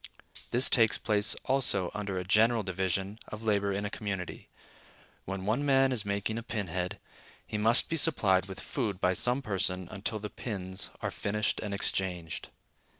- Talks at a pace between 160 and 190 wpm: Yes, average, 170 wpm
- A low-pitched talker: Yes, low, 105 Hz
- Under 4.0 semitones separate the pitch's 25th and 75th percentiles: Yes, average, 2.9 semitones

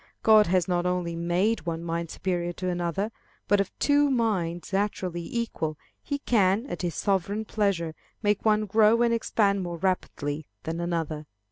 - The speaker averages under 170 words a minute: Yes, average, 160 wpm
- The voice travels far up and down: No, average, 3.9 semitones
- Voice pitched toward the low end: No, medium, 185 Hz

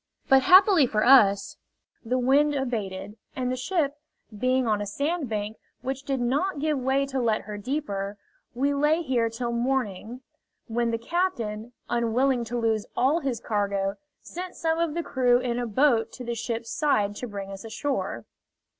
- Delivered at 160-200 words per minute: Yes, average, 170 wpm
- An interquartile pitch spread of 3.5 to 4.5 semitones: Yes, average, 4.1 semitones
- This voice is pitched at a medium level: No, high, 245 Hz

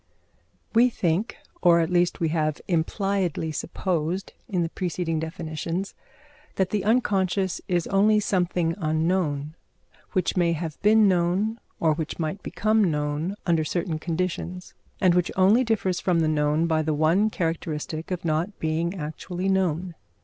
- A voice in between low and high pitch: Yes, medium, 175 Hz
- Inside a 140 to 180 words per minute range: Yes, average, 145 wpm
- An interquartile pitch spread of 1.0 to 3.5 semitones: Yes, average, 3.1 semitones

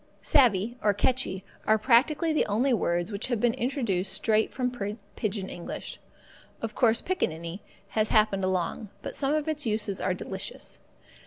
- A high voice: Yes, high, 215 Hz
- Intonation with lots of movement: No, average, 4.5 semitones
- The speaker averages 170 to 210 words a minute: No, average, 155 wpm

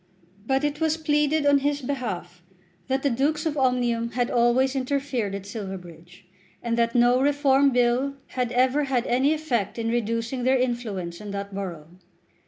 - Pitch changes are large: No, average, 3.6 semitones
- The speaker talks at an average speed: Yes, average, 165 wpm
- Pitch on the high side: Yes, high, 245 Hz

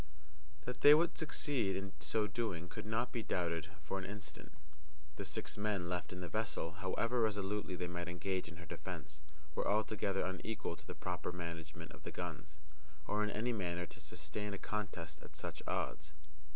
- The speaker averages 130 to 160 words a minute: No, average, 180 wpm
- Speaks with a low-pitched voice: Yes, very low, 95 Hz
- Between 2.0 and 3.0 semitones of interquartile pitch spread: No, average, 3.6 semitones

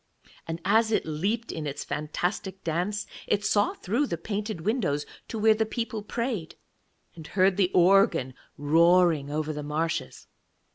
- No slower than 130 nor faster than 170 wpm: Yes, average, 150 wpm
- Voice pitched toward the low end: No, medium, 185 Hz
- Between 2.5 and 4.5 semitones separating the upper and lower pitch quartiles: No, average, 5.2 semitones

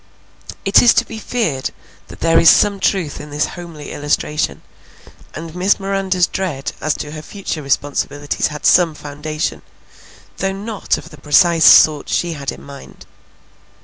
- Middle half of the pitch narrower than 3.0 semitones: No, average, 4.4 semitones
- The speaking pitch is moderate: Yes, medium, 160 Hz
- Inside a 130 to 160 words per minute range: Yes, average, 155 wpm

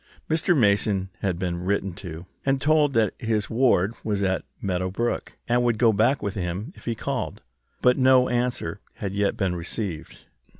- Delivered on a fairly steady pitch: No, average, 4.5 semitones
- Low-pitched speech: Yes, low, 105 Hz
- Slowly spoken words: No, average, 175 wpm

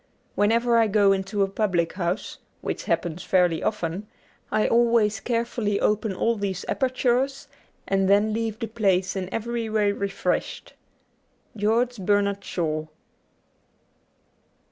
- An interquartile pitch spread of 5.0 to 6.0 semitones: No, average, 3.0 semitones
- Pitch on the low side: No, high, 205 Hz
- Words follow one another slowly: Yes, slow, 125 wpm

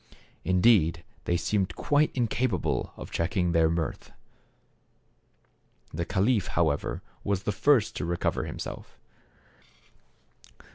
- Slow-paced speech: Yes, slow, 100 wpm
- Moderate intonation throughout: Yes, average, 4.1 semitones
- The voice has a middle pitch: No, very low, 95 Hz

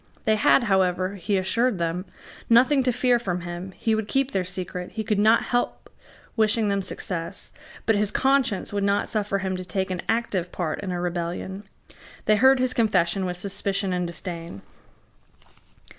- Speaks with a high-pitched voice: Yes, high, 195 Hz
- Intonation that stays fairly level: No, average, 3.5 semitones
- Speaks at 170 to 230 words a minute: Yes, average, 175 wpm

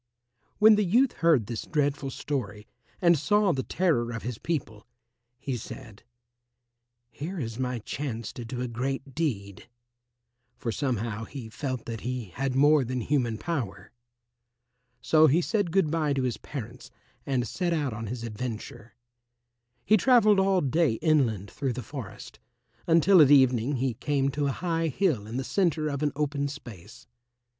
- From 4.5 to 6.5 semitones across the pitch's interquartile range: Yes, average, 5.0 semitones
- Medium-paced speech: Yes, average, 160 wpm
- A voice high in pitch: No, low, 135 Hz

